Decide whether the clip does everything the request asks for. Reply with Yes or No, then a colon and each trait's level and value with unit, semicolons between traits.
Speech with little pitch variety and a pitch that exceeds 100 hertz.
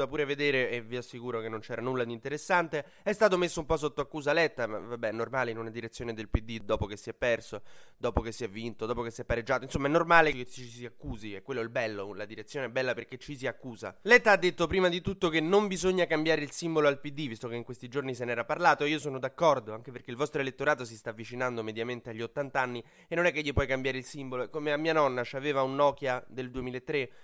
No: average, 4.3 semitones; low, 130 Hz